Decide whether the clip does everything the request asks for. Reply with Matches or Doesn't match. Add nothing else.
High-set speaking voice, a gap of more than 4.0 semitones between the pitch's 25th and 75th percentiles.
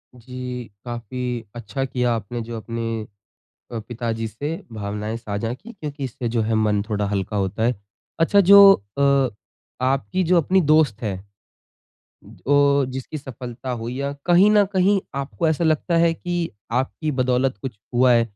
Doesn't match